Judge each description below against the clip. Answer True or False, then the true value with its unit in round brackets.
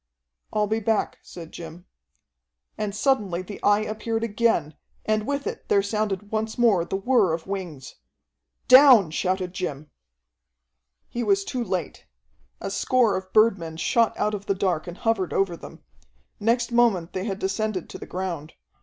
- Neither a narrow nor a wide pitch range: True (3.6 semitones)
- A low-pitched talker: False (200 Hz)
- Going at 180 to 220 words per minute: False (160 wpm)